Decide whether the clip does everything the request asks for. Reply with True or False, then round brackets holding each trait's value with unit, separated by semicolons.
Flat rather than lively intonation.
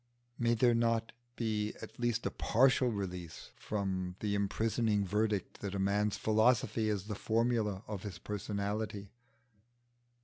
True (2.2 semitones)